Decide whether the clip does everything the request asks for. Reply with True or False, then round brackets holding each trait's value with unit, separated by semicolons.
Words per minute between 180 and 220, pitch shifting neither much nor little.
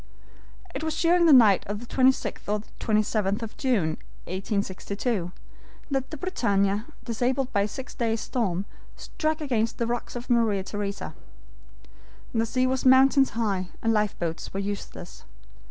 False (145 wpm; 4.4 semitones)